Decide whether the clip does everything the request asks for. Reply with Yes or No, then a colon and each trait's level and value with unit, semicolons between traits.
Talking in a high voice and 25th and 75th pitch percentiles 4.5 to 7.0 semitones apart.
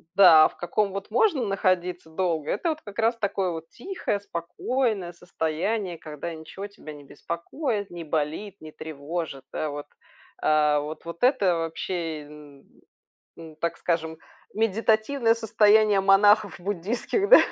No: medium, 180 Hz; average, 4.8 semitones